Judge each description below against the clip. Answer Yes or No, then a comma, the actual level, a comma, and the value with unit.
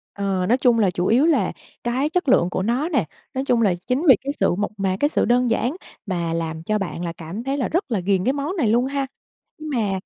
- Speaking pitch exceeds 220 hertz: Yes, high, 235 Hz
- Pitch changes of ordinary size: No, wide, 6.2 semitones